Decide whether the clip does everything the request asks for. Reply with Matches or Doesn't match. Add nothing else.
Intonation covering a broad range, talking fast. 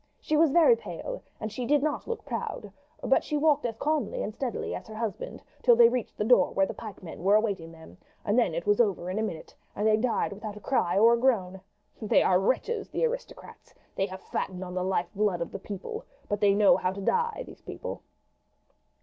Matches